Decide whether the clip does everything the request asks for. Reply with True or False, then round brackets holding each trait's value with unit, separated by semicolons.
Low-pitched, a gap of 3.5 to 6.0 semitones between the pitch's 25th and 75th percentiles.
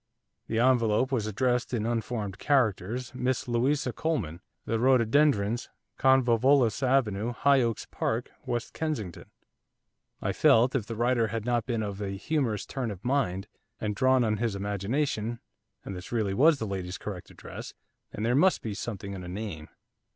True (115 Hz; 3.9 semitones)